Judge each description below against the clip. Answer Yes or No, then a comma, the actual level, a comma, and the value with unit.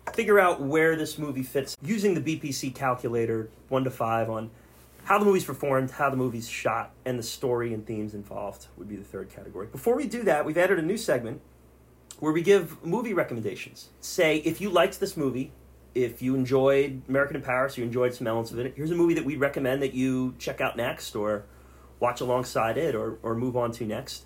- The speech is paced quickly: Yes, fast, 215 wpm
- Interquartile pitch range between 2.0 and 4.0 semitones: No, average, 5.1 semitones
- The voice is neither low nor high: No, low, 130 Hz